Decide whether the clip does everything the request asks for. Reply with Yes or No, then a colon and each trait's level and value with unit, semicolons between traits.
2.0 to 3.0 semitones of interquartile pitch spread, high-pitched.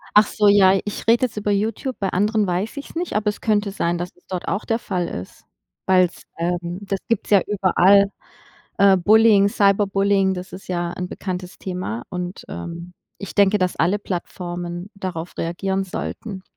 Yes: narrow, 2.4 semitones; high, 195 Hz